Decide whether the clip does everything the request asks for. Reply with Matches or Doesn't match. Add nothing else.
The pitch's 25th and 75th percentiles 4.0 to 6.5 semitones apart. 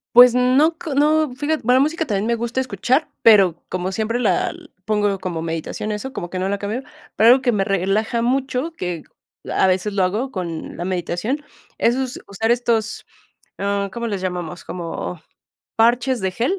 Matches